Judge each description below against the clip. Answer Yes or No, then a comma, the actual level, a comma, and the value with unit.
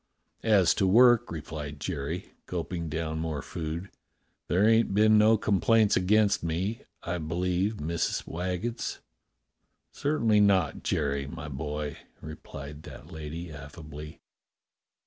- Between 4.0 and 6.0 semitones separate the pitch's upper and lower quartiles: Yes, average, 5.2 semitones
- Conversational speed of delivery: No, slow, 115 wpm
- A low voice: Yes, very low, 85 Hz